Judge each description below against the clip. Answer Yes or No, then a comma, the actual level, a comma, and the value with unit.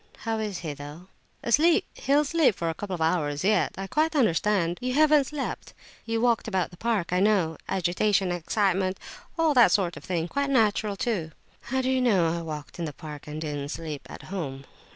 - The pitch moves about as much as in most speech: No, wide, 6.2 semitones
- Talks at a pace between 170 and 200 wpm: Yes, average, 175 wpm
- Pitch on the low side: No, high, 195 Hz